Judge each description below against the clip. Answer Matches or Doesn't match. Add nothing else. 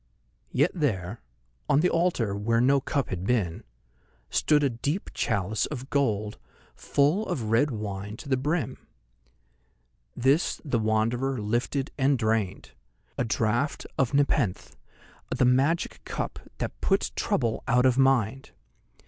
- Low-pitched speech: Matches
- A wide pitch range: Doesn't match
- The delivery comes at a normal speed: Doesn't match